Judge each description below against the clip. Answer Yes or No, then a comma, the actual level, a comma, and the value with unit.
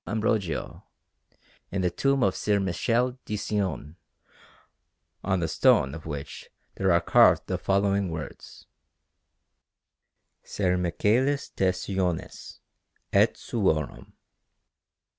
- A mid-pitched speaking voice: No, very low, 95 Hz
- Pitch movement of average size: Yes, average, 3.6 semitones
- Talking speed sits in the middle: No, slow, 105 wpm